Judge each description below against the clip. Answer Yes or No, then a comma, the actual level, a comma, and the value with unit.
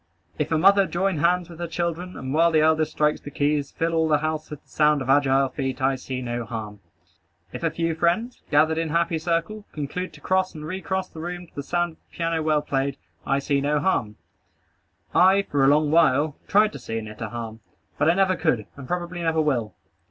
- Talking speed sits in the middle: No, fast, 230 wpm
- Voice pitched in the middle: Yes, medium, 155 Hz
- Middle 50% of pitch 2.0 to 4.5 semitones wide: Yes, average, 3.6 semitones